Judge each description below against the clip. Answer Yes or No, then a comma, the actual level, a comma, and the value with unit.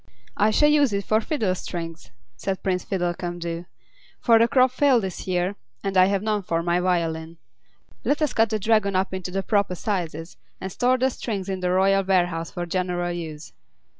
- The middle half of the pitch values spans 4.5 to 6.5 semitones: No, average, 3.5 semitones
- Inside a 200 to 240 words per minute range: No, average, 190 wpm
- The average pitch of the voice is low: No, high, 190 Hz